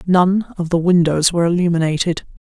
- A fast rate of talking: No, average, 145 wpm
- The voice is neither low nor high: Yes, medium, 175 Hz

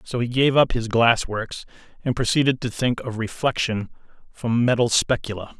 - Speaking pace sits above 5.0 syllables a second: No, 4.9 syllables/s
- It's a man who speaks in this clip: Yes, male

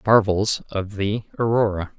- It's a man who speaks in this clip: Yes, male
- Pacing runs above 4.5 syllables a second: No, 4.3 syllables/s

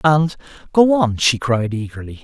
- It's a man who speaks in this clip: Yes, male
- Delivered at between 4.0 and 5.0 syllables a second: Yes, 4.6 syllables/s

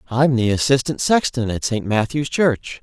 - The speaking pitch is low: Yes, low, 125 Hz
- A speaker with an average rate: Yes, average, 170 wpm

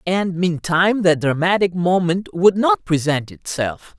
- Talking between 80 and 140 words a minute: Yes, slow, 135 wpm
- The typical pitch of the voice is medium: Yes, medium, 180 Hz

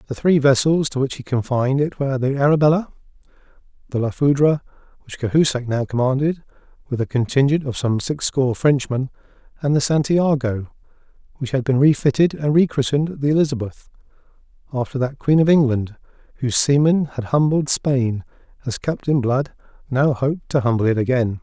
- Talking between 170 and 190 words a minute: No, average, 155 wpm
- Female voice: No, male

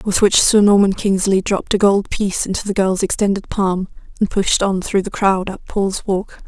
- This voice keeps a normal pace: No, fast, 215 wpm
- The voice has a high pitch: Yes, high, 195 Hz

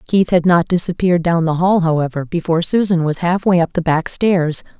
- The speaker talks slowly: No, average, 200 wpm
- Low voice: No, medium, 170 Hz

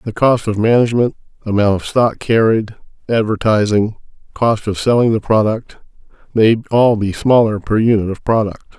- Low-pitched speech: Yes, low, 110 Hz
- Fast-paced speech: No, average, 150 wpm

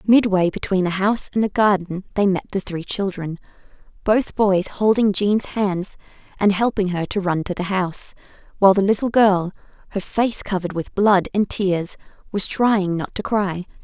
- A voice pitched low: No, high, 195 Hz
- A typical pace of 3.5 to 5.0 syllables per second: Yes, 4.8 syllables/s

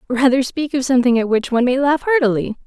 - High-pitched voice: Yes, very high, 260 Hz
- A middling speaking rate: No, fast, 225 wpm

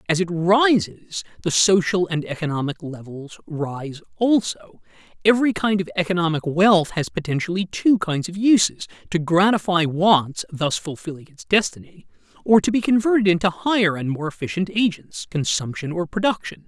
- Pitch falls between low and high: Yes, medium, 175 Hz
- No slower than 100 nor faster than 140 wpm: Yes, slow, 135 wpm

